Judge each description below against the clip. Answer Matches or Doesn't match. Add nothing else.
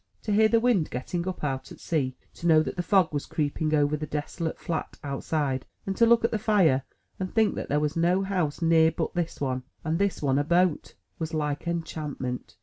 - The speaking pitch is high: Doesn't match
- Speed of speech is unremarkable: Doesn't match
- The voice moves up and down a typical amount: Matches